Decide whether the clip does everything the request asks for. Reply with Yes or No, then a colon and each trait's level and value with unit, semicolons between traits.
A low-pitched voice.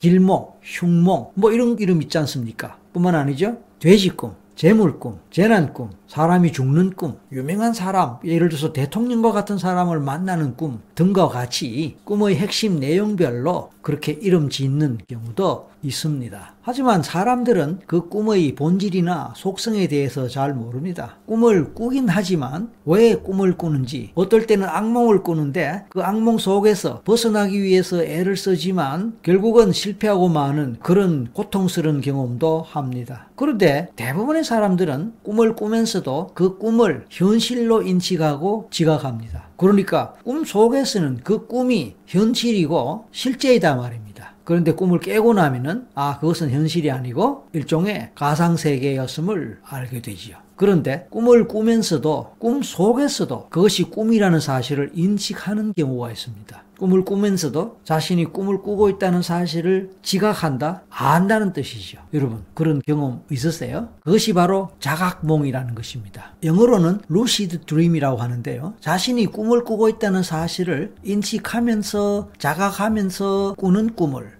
No: medium, 180 Hz